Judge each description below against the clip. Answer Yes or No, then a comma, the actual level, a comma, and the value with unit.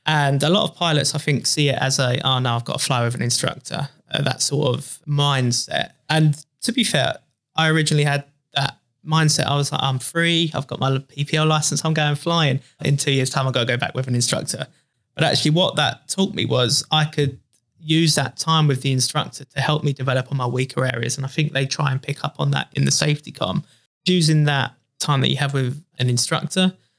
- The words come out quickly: Yes, fast, 235 wpm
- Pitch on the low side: No, medium, 145 Hz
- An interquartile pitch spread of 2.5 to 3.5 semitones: Yes, average, 3.0 semitones